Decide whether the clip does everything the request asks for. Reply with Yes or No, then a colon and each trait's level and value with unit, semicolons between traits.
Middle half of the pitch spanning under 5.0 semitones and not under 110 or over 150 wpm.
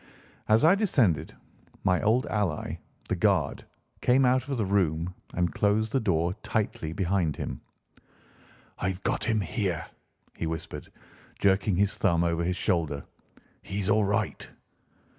Yes: average, 4.3 semitones; average, 140 wpm